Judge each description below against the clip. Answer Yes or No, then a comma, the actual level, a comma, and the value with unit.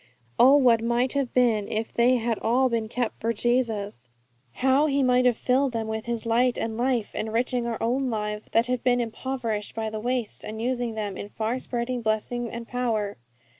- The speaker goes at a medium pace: Yes, average, 195 wpm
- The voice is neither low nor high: No, high, 235 Hz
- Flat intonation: Yes, narrow, 2.2 semitones